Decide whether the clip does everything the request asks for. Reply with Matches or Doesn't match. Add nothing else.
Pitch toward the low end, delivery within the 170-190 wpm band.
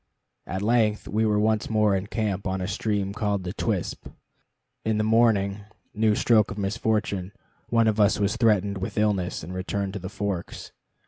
Matches